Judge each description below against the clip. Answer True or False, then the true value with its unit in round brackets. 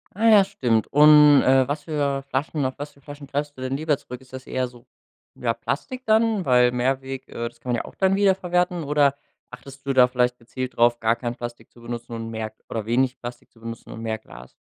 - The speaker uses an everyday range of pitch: True (3.6 semitones)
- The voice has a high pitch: False (130 Hz)